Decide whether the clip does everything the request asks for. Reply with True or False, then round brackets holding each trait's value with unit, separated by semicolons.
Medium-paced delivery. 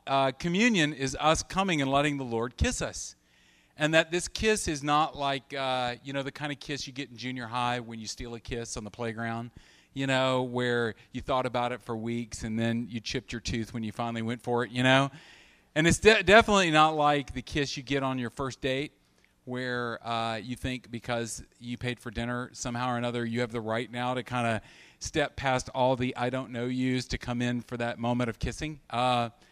False (230 wpm)